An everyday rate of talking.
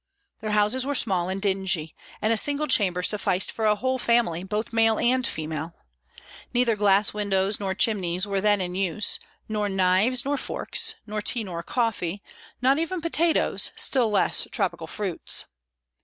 Yes: average, 160 wpm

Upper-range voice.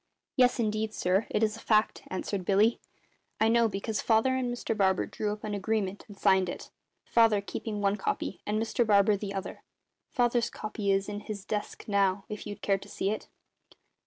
Yes: high, 210 Hz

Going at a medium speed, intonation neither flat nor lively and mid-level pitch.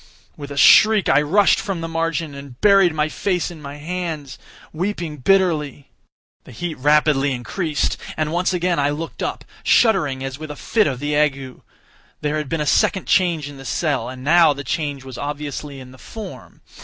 Yes: average, 180 wpm; average, 3.6 semitones; medium, 150 Hz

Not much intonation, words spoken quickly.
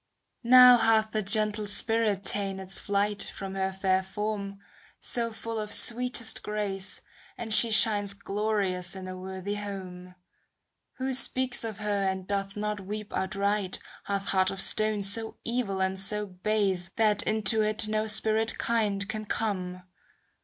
No: narrow, 2.0 semitones; average, 155 wpm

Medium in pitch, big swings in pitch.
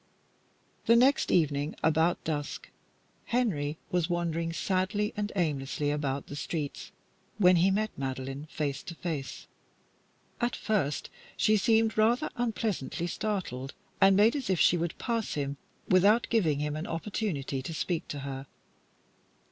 Yes: medium, 170 Hz; wide, 6.4 semitones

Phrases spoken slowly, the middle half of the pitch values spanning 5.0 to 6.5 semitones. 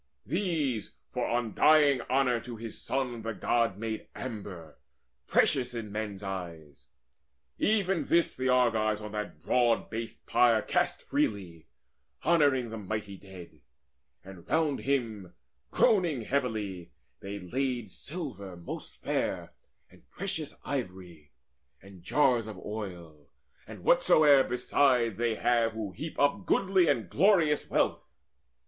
Yes: slow, 125 wpm; wide, 5.5 semitones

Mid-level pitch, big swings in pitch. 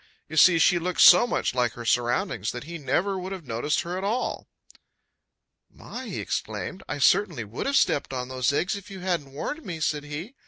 Yes: medium, 165 Hz; wide, 6.4 semitones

